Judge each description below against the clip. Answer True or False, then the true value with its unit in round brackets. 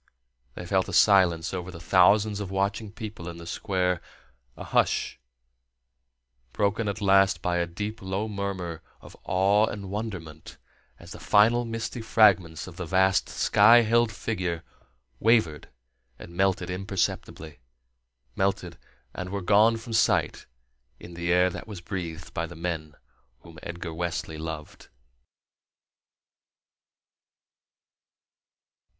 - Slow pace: True (125 wpm)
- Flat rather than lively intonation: False (3.2 semitones)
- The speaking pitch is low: True (95 Hz)